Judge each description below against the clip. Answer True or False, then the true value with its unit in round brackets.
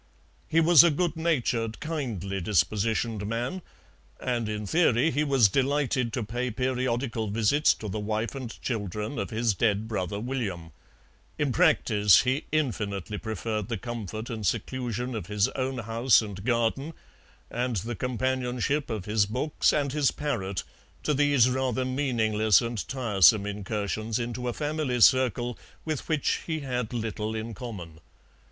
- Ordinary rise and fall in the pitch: True (3.6 semitones)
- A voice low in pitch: True (120 Hz)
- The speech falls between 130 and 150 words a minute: True (145 wpm)